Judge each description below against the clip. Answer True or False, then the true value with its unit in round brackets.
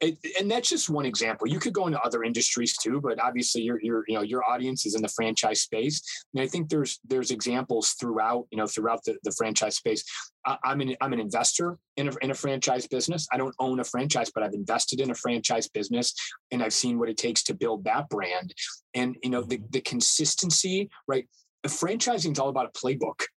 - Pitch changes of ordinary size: True (4.2 semitones)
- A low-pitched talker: True (130 Hz)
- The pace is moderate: False (220 wpm)